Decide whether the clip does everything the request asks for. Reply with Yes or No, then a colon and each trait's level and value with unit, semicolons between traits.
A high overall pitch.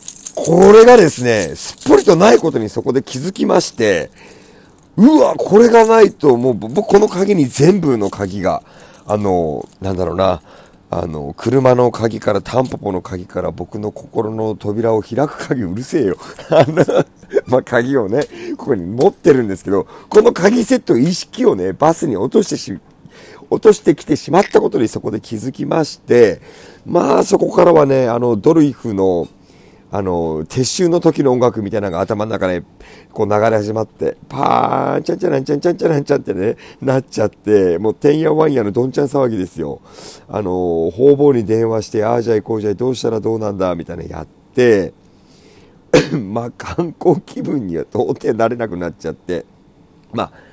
No: low, 120 Hz